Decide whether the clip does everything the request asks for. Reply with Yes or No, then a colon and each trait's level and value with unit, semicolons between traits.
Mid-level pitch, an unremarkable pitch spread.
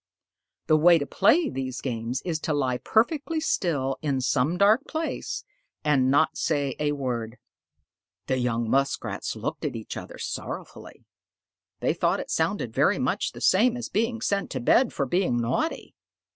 No: medium, 145 Hz; wide, 7.7 semitones